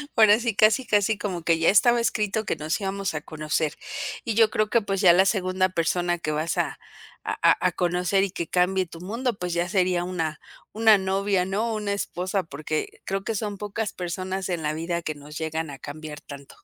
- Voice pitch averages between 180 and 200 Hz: Yes, medium, 185 Hz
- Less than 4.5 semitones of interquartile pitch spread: Yes, average, 3.9 semitones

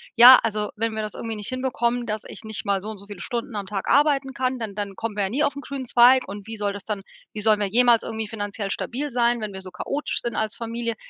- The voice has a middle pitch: No, high, 225 Hz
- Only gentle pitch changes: No, average, 3.0 semitones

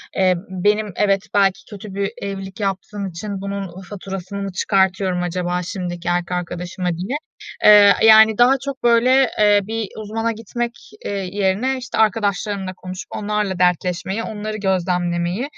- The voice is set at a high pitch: Yes, high, 195 Hz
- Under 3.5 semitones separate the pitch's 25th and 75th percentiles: Yes, average, 2.7 semitones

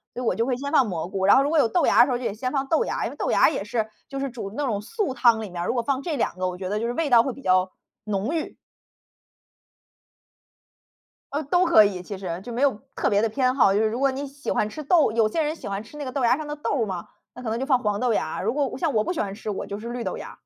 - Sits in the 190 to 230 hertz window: No, high, 240 Hz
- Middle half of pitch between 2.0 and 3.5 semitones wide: No, average, 5.0 semitones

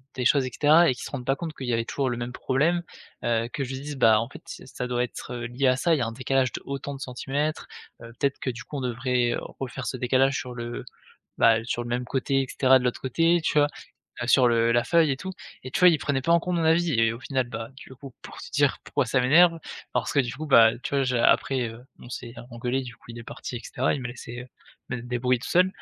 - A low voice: Yes, low, 130 Hz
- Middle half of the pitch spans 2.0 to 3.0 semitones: Yes, average, 2.7 semitones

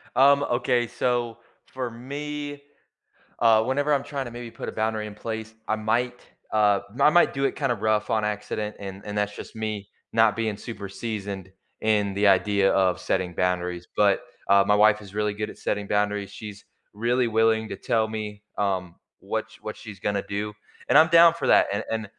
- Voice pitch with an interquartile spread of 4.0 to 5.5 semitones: No, average, 2.8 semitones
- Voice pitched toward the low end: Yes, low, 110 Hz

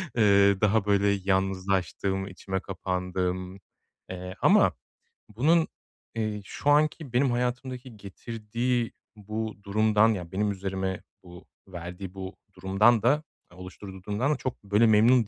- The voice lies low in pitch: Yes, low, 100 Hz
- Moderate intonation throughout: Yes, average, 3.5 semitones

